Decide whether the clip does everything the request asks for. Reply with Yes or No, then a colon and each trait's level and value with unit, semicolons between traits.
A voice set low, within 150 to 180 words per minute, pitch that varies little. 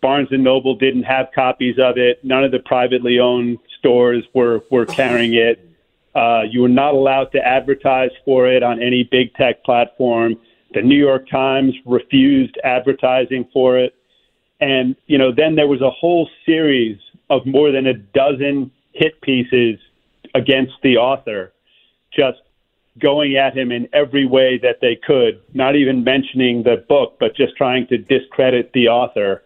Yes: low, 130 Hz; average, 165 wpm; narrow, 1.7 semitones